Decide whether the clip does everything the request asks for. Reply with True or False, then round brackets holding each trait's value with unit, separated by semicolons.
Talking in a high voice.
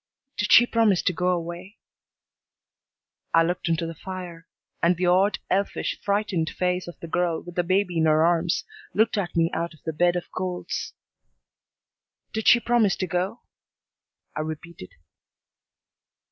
False (175 Hz)